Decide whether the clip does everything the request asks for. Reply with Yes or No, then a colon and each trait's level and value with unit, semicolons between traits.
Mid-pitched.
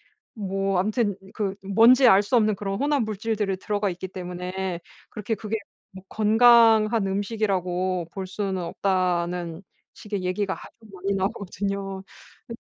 No: high, 195 Hz